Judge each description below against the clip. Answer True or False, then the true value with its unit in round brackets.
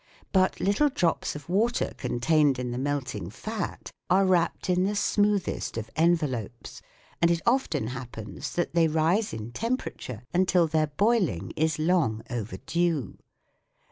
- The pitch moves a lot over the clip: True (6.8 semitones)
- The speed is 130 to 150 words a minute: True (140 wpm)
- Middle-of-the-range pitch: True (165 Hz)